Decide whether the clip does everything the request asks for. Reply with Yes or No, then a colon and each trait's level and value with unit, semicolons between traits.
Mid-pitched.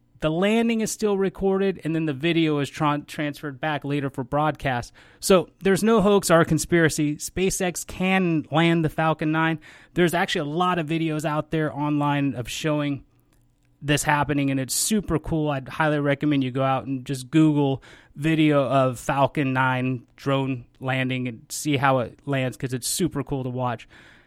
Yes: medium, 150 Hz